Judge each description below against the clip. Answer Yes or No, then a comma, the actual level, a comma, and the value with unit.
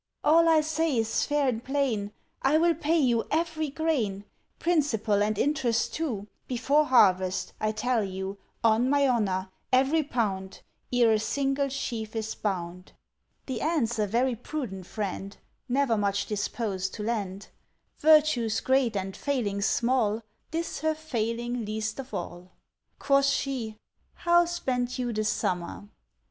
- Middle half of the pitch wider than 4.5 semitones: Yes, average, 5.2 semitones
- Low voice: No, high, 235 Hz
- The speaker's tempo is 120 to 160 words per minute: Yes, average, 140 wpm